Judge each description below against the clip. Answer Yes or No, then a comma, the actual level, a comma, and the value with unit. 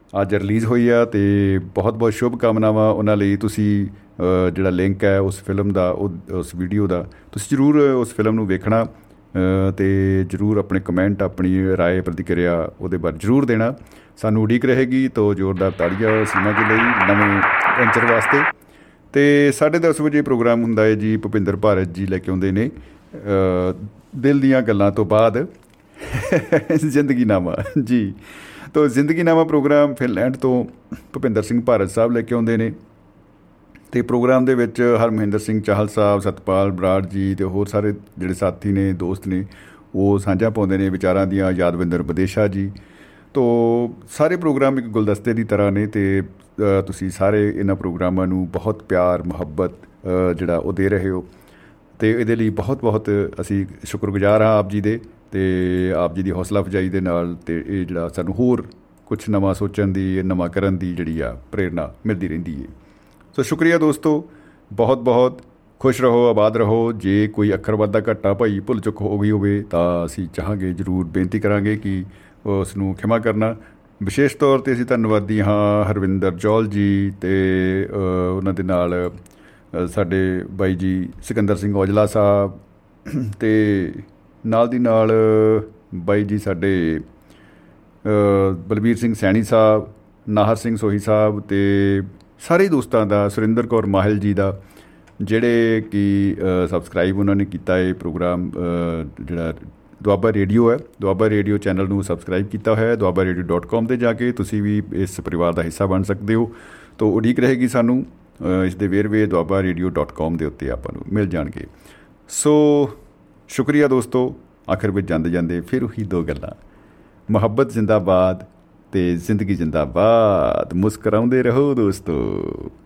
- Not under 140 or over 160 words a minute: Yes, average, 155 wpm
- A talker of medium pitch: No, low, 100 Hz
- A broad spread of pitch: No, average, 3.1 semitones